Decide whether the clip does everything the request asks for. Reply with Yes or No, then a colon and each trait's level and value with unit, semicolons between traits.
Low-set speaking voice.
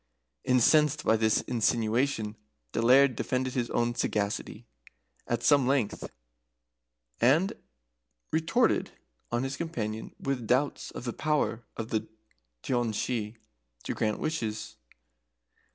Yes: low, 120 Hz